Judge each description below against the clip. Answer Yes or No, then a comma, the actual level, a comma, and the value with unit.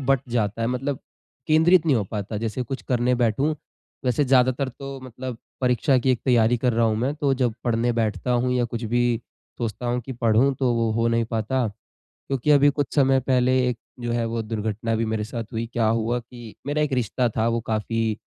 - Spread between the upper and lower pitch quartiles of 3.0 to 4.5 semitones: No, narrow, 2.4 semitones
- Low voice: Yes, low, 120 Hz